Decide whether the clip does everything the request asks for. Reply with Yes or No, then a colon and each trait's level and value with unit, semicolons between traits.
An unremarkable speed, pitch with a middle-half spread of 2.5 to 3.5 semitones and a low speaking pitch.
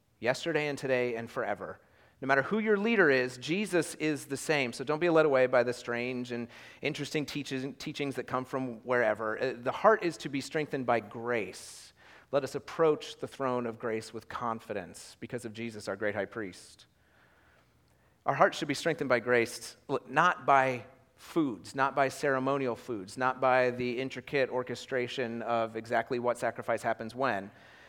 Yes: average, 170 wpm; average, 3.2 semitones; low, 130 Hz